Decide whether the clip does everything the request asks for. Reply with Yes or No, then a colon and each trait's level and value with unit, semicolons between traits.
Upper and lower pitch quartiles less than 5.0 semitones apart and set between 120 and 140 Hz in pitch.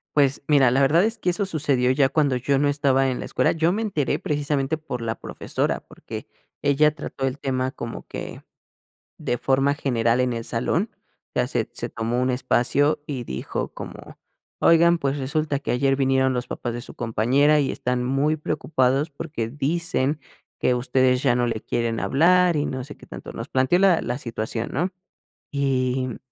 Yes: average, 3.1 semitones; low, 135 Hz